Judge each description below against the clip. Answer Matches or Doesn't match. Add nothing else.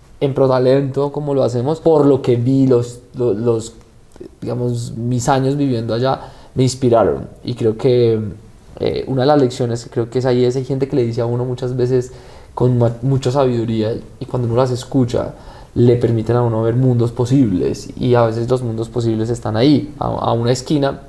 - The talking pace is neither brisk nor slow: Doesn't match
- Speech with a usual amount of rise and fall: Doesn't match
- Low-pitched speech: Matches